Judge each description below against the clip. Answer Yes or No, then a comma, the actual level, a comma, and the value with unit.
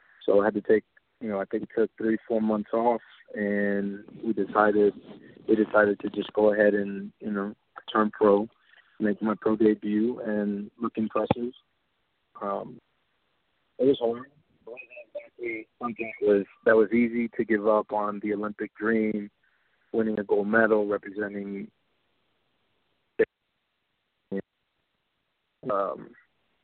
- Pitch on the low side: Yes, low, 105 Hz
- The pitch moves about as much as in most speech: No, narrow, 1.5 semitones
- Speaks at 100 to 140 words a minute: Yes, slow, 135 wpm